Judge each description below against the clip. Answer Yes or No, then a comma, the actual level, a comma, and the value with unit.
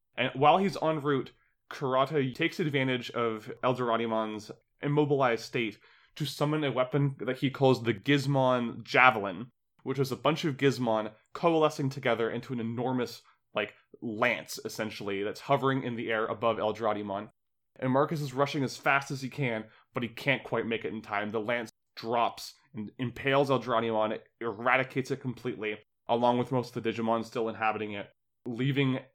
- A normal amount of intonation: Yes, average, 3.4 semitones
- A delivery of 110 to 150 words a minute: No, average, 165 wpm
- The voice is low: Yes, low, 125 Hz